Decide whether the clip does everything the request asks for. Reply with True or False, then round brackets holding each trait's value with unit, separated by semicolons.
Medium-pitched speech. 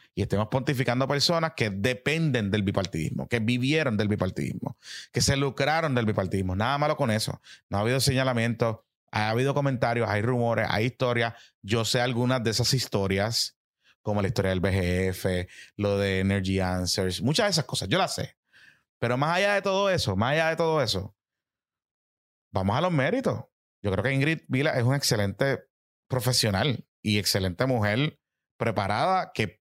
False (120 Hz)